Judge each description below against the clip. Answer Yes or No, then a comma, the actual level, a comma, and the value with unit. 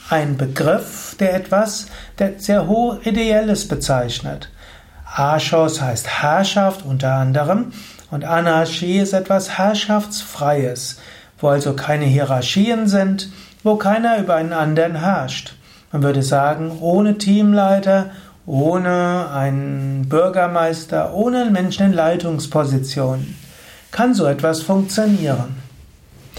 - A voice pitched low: No, medium, 165 Hz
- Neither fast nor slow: No, slow, 105 wpm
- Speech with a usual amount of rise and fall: No, wide, 5.9 semitones